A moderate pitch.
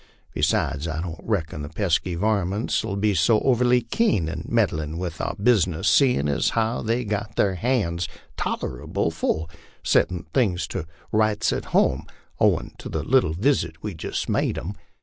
No: very low, 95 Hz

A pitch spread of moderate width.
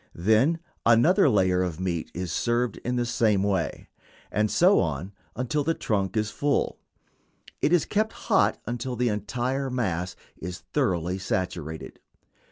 No: wide, 5.8 semitones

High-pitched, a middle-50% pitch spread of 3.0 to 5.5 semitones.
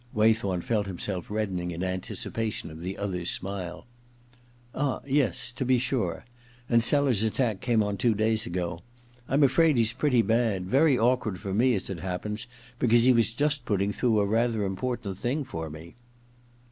No: low, 110 Hz; average, 4.4 semitones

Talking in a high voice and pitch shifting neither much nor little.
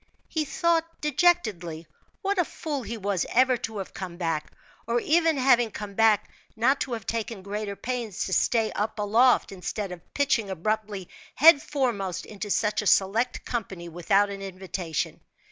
Yes: high, 215 Hz; average, 4.7 semitones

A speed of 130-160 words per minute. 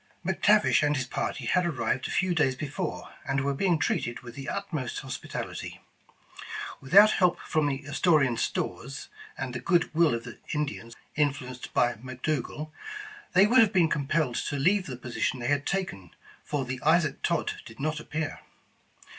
No: average, 170 wpm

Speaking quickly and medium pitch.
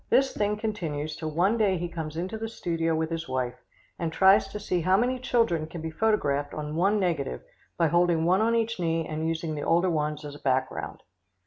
Yes: fast, 220 wpm; medium, 170 Hz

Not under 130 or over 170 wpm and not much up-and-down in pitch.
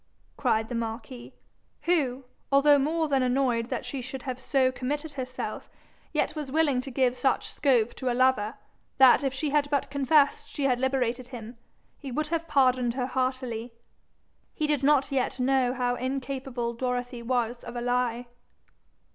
Yes: average, 165 wpm; narrow, 2.1 semitones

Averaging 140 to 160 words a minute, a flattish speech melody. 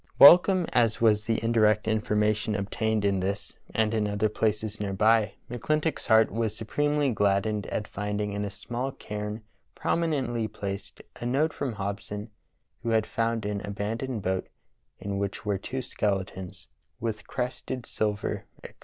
Yes: average, 155 wpm; narrow, 2.2 semitones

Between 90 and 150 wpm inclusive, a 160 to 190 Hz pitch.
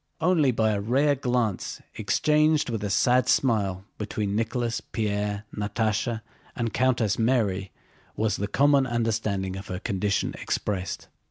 No: slow, 135 wpm; low, 110 Hz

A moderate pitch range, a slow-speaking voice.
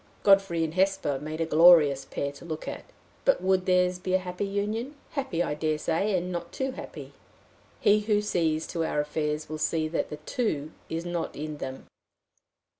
No: average, 3.8 semitones; average, 190 wpm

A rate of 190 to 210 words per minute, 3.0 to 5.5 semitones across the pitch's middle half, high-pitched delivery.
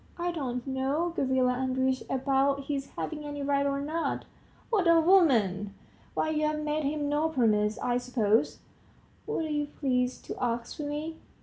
No: average, 170 wpm; average, 3.3 semitones; very high, 280 Hz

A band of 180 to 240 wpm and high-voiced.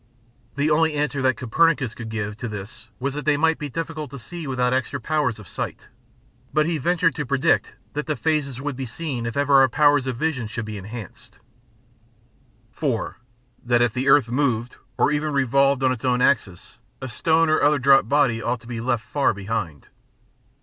No: average, 195 wpm; low, 135 Hz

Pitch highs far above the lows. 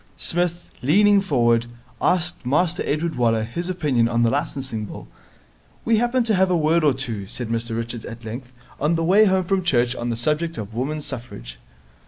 Yes: wide, 6.8 semitones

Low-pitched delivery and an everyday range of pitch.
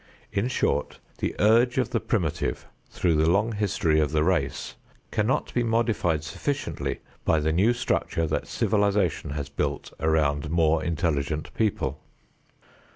No: very low, 85 Hz; wide, 5.7 semitones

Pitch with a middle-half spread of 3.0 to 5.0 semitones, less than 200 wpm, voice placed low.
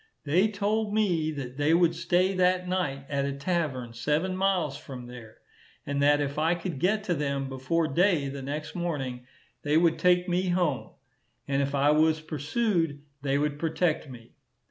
No: average, 4.3 semitones; average, 175 wpm; medium, 155 Hz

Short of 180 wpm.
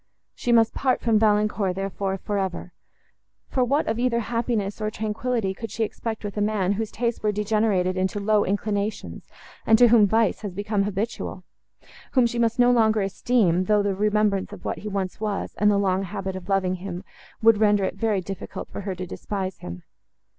No: average, 190 wpm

